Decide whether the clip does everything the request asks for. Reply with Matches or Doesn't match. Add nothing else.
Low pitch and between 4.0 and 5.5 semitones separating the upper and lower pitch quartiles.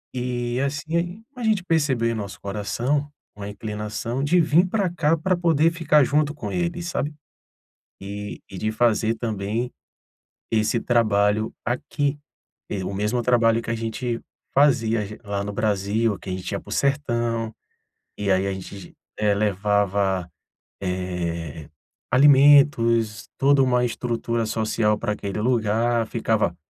Matches